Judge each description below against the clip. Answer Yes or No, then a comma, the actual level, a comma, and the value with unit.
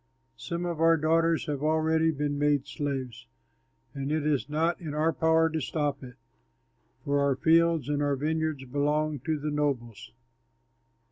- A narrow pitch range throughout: Yes, narrow, 2.1 semitones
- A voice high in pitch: No, medium, 150 Hz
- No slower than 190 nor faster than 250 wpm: No, average, 155 wpm